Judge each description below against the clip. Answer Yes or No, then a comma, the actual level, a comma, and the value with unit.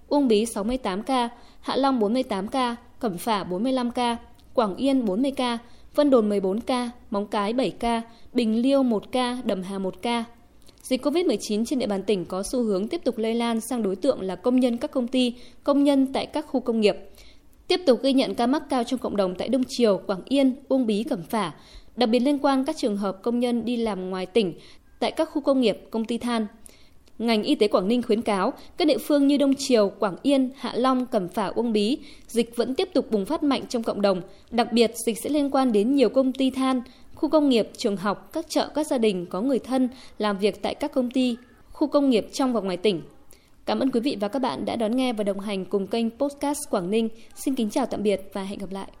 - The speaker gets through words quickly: No, average, 240 wpm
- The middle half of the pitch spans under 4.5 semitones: Yes, average, 3.9 semitones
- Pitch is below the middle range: No, high, 240 Hz